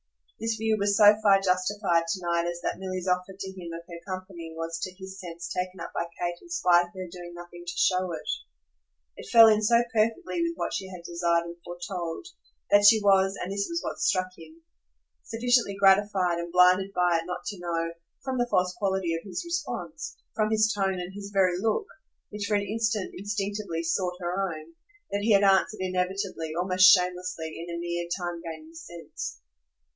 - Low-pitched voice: No, medium, 185 Hz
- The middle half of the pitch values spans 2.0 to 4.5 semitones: Yes, average, 2.8 semitones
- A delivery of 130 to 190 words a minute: No, average, 200 wpm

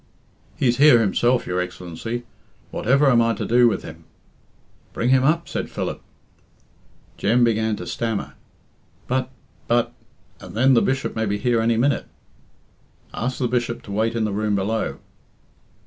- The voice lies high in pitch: No, low, 115 Hz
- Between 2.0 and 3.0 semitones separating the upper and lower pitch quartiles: Yes, narrow, 2.5 semitones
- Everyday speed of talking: Yes, average, 155 wpm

